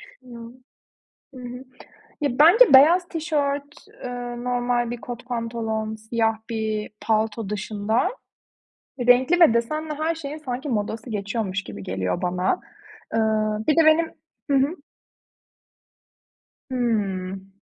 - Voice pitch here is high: Yes, high, 240 Hz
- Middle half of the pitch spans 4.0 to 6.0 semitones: Yes, average, 4.5 semitones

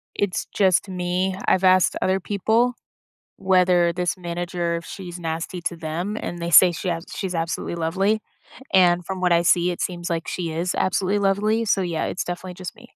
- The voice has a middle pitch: Yes, medium, 180 Hz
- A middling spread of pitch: No, narrow, 1.8 semitones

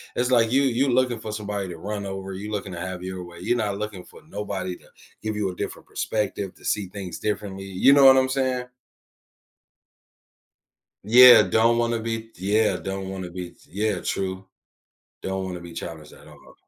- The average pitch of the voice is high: No, low, 100 Hz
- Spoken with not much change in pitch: No, average, 3.4 semitones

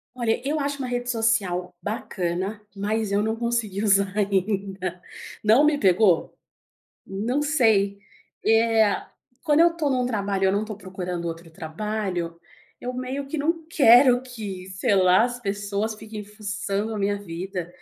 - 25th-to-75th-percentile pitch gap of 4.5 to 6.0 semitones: No, average, 4.0 semitones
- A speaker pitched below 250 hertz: Yes, high, 210 Hz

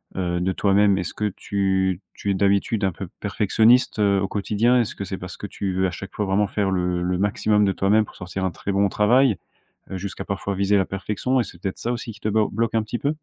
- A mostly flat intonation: Yes, narrow, 1.9 semitones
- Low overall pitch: Yes, low, 100 Hz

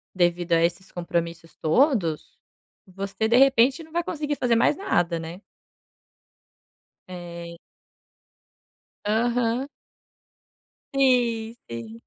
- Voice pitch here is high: Yes, high, 200 Hz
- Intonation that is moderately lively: No, wide, 6.5 semitones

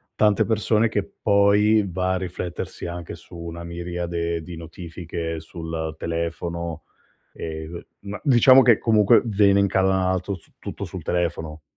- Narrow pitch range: No, average, 3.2 semitones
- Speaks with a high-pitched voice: No, very low, 90 Hz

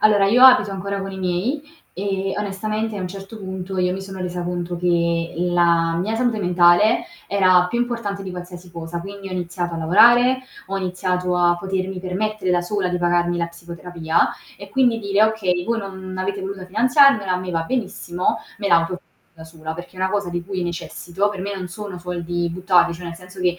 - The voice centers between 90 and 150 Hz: No, medium, 185 Hz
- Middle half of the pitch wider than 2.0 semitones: Yes, narrow, 2.4 semitones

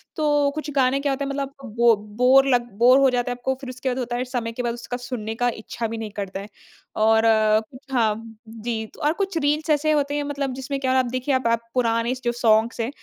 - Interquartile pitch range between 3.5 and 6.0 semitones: No, average, 3.0 semitones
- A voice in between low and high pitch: No, very high, 250 Hz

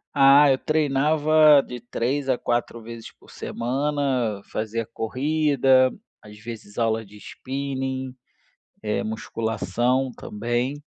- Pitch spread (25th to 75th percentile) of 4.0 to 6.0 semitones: No, average, 3.5 semitones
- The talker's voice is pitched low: Yes, low, 130 Hz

